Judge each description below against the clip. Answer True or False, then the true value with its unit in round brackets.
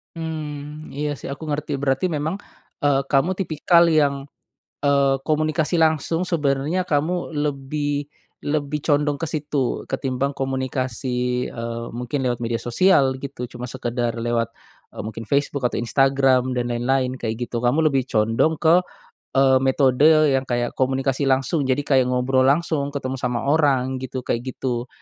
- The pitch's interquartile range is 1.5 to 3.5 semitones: True (2.9 semitones)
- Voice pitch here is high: False (135 Hz)